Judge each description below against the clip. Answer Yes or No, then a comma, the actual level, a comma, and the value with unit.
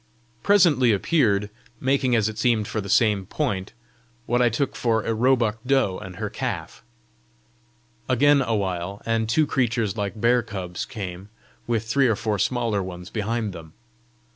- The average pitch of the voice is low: Yes, low, 110 Hz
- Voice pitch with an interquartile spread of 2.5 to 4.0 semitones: Yes, average, 3.7 semitones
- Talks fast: No, average, 160 wpm